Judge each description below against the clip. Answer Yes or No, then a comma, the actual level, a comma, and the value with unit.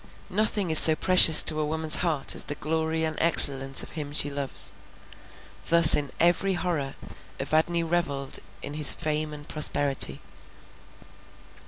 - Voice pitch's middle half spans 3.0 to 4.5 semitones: No, narrow, 2.6 semitones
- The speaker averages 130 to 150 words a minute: Yes, average, 145 wpm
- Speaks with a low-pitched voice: No, medium, 155 Hz